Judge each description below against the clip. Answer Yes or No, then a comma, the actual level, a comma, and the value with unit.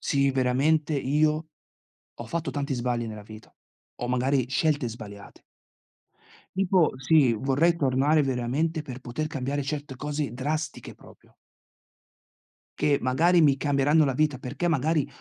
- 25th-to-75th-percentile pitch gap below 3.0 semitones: No, average, 3.3 semitones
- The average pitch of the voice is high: No, medium, 140 Hz